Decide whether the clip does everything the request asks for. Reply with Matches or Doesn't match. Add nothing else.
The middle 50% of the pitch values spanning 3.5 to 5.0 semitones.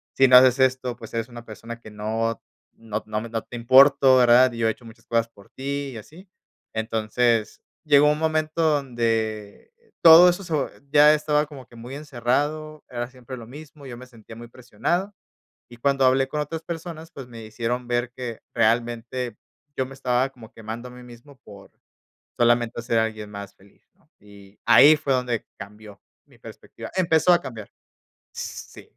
Matches